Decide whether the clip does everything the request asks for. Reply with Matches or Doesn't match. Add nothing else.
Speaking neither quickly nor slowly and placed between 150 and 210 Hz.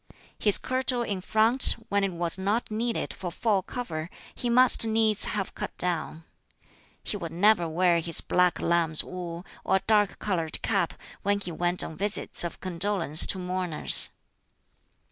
Matches